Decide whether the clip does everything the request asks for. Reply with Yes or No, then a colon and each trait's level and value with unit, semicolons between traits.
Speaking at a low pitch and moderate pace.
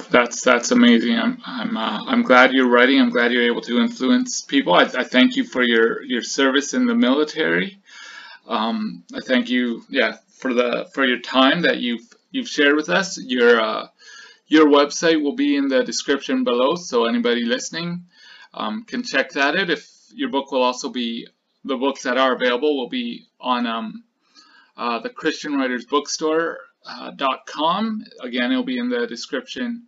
No: medium, 165 Hz; average, 185 wpm